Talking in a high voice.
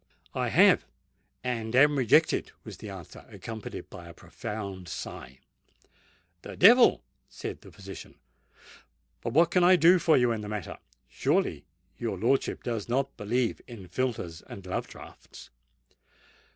No: low, 115 Hz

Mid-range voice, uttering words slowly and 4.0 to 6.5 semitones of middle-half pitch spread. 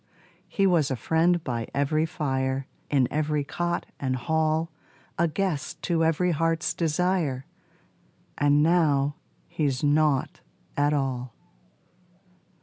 No: medium, 150 Hz; slow, 115 wpm; average, 3.1 semitones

